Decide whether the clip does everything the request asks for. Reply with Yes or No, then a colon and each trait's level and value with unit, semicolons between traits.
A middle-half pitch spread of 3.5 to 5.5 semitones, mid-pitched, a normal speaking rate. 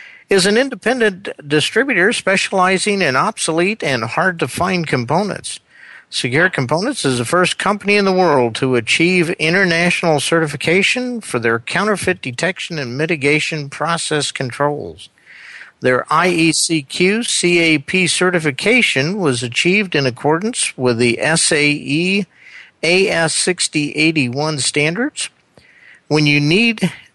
No: average, 4.5 semitones; medium, 165 Hz; slow, 110 wpm